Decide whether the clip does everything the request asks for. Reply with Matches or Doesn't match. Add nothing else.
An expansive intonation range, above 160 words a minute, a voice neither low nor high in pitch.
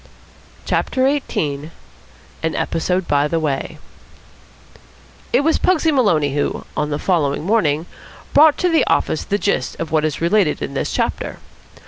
Doesn't match